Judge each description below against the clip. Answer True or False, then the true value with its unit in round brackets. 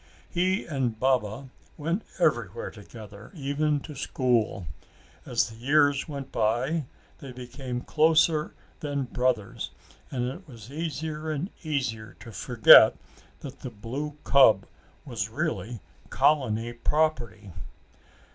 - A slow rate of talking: True (115 wpm)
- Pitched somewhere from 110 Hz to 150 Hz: True (135 Hz)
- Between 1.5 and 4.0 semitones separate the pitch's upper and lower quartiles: False (4.4 semitones)